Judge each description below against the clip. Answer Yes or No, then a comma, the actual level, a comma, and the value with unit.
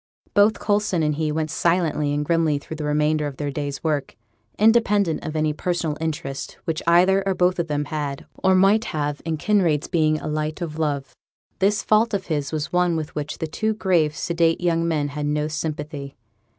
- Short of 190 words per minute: No, average, 195 wpm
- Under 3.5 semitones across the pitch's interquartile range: Yes, average, 3.1 semitones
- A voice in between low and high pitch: Yes, medium, 155 Hz